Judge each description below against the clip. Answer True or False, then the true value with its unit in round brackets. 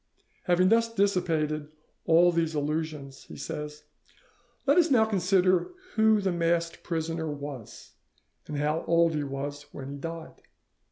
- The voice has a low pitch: False (165 Hz)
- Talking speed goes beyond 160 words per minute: False (135 wpm)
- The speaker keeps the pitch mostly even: False (3.7 semitones)